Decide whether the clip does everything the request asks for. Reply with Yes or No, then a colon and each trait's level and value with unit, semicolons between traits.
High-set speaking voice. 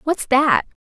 Yes: very high, 280 Hz